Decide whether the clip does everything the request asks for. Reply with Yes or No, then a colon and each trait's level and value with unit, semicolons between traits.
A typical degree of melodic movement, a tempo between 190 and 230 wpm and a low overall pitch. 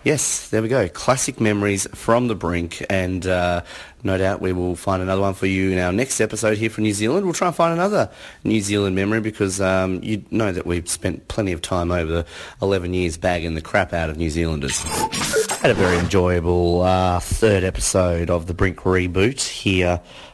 Yes: average, 3.2 semitones; fast, 205 wpm; very low, 95 Hz